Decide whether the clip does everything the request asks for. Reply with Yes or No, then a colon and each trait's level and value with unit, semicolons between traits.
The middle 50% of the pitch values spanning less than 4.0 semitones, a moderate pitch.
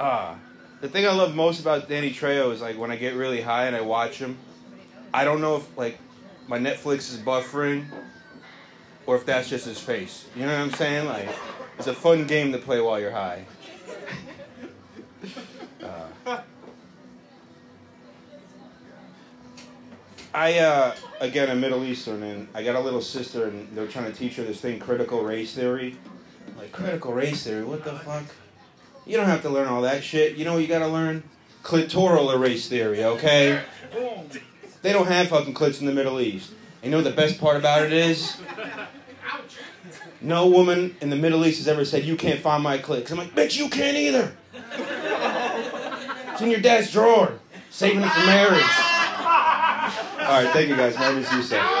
No: average, 4.7 semitones; medium, 150 Hz